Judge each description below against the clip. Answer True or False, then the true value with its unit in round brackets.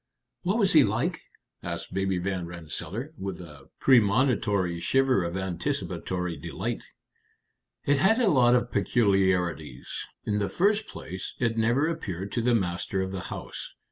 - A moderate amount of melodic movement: False (6.1 semitones)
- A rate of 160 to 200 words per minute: False (145 wpm)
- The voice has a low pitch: True (100 Hz)